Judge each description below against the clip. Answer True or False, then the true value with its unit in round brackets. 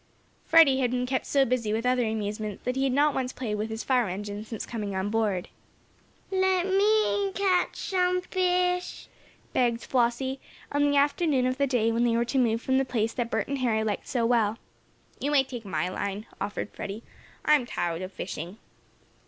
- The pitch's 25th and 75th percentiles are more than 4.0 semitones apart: True (4.5 semitones)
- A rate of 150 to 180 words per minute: False (195 wpm)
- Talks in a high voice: True (245 Hz)